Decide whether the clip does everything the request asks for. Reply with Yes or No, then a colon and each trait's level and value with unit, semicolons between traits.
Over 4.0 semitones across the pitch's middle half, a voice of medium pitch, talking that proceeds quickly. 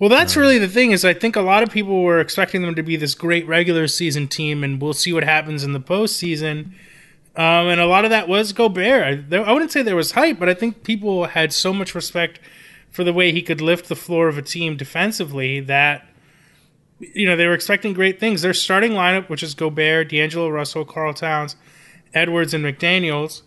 No: average, 3.5 semitones; medium, 170 Hz; fast, 220 wpm